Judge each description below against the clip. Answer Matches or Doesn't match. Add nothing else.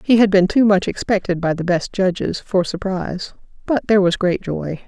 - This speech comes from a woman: Matches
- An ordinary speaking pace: Matches